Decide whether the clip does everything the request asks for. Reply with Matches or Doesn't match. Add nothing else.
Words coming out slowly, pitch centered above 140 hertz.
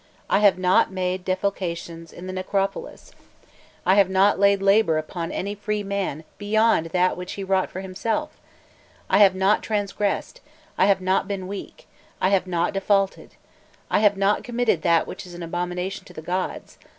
Doesn't match